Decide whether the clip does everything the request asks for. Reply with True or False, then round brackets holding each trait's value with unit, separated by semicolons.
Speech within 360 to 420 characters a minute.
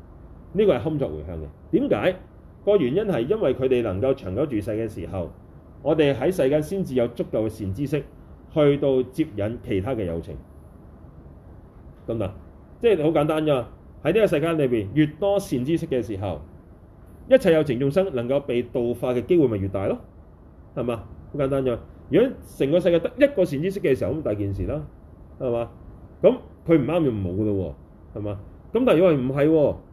False (275 characters per minute)